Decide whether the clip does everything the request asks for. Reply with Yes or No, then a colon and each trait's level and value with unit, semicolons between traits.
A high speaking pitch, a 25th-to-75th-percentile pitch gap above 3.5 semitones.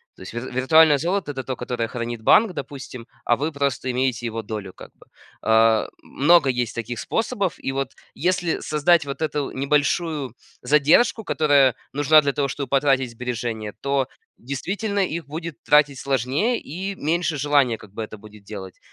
No: medium, 140 Hz; average, 4.4 semitones